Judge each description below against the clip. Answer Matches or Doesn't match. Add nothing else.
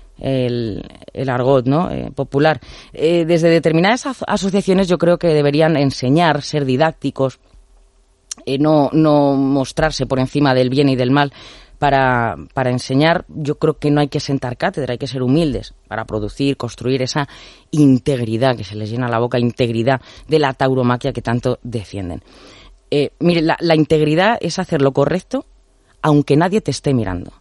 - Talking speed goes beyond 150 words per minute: Matches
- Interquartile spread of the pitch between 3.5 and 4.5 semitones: Matches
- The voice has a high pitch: Doesn't match